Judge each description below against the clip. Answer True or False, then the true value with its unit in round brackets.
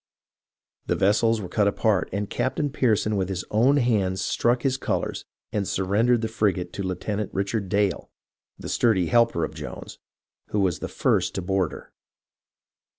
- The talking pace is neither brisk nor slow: True (165 wpm)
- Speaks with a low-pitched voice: True (105 Hz)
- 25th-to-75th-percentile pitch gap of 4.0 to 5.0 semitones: False (3.2 semitones)